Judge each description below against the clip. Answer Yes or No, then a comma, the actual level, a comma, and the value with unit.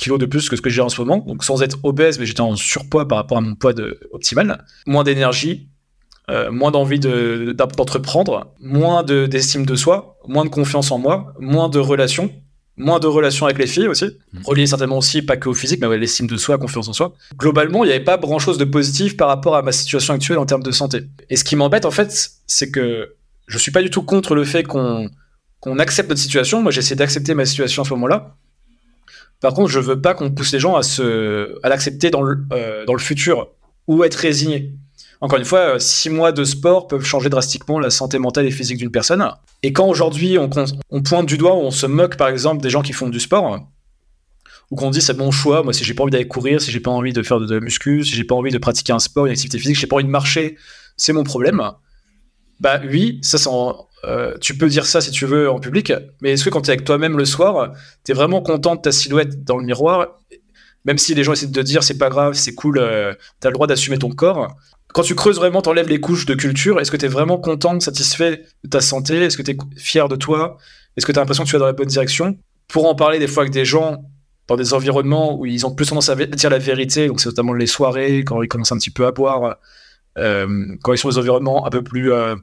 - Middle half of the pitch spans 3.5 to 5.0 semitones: No, average, 3.1 semitones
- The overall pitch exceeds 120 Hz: Yes, medium, 140 Hz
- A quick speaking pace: Yes, fast, 260 wpm